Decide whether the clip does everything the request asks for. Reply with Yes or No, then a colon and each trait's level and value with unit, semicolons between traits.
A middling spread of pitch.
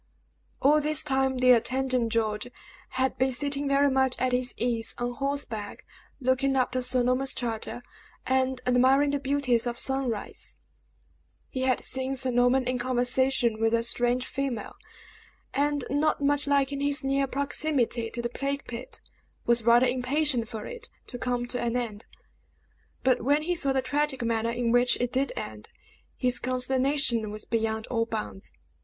No: narrow, 2.3 semitones